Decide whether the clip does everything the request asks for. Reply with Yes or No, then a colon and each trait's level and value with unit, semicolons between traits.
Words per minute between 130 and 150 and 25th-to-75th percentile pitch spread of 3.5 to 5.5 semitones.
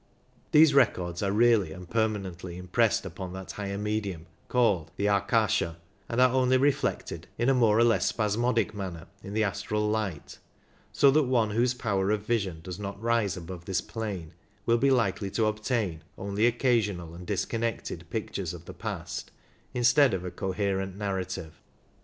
No: average, 165 wpm; average, 3.9 semitones